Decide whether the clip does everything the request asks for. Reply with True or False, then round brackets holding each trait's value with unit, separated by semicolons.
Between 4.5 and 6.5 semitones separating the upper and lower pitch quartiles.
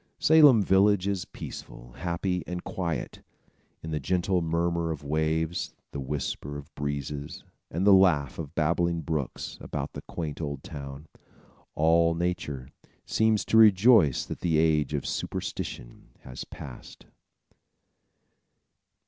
False (3.8 semitones)